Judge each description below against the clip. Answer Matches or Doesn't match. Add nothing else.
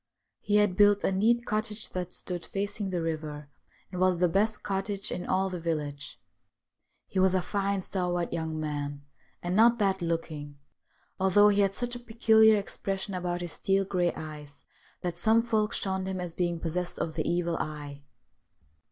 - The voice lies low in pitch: Doesn't match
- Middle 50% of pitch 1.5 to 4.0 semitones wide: Matches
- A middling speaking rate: Matches